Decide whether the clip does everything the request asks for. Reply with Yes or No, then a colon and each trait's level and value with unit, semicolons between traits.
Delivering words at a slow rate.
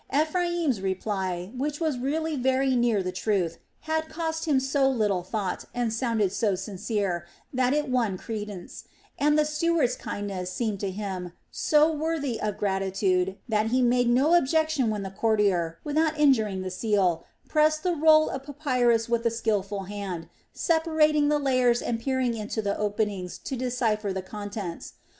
No: average, 160 wpm